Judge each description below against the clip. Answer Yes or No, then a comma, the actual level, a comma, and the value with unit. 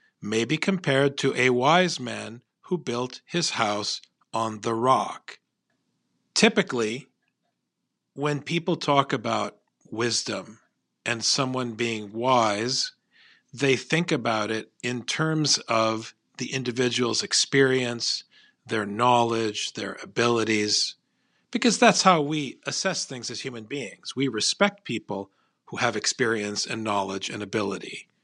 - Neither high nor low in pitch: No, low, 125 Hz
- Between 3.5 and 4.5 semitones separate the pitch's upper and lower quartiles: Yes, average, 4.2 semitones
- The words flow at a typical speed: No, slow, 120 wpm